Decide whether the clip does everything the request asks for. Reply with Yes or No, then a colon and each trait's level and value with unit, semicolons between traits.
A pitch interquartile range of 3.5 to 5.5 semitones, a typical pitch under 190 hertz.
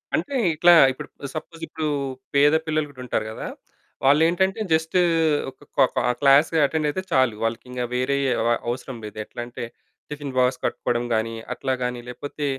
Yes: average, 4.0 semitones; medium, 140 Hz